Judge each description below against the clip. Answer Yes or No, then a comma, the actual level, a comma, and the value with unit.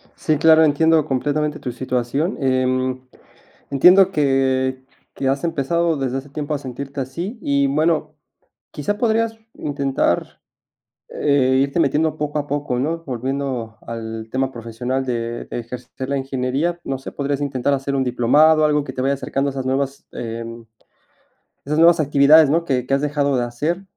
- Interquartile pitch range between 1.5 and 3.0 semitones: Yes, average, 2.7 semitones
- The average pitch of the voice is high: No, medium, 140 Hz